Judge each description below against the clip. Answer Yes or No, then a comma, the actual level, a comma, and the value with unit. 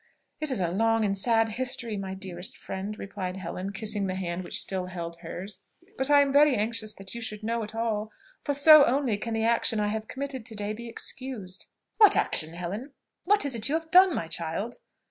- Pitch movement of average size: Yes, average, 4.9 semitones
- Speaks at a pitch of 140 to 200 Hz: No, high, 215 Hz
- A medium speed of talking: No, fast, 215 wpm